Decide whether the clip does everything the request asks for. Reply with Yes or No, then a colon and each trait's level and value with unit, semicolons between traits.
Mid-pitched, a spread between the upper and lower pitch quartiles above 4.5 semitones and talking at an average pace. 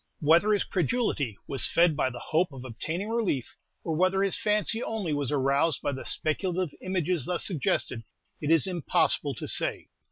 Yes: medium, 165 Hz; average, 5.1 semitones; average, 170 wpm